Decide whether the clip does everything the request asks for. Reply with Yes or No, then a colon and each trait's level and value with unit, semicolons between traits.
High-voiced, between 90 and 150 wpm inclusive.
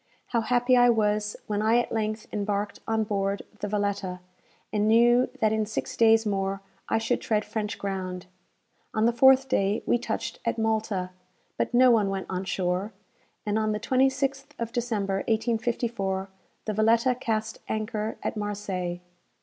No: high, 215 Hz; average, 160 wpm